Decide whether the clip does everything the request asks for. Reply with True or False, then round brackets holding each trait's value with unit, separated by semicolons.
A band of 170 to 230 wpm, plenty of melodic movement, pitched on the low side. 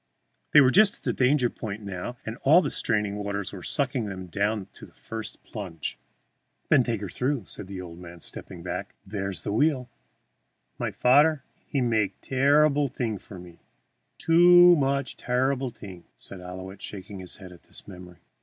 True (180 wpm; 6.1 semitones; 110 Hz)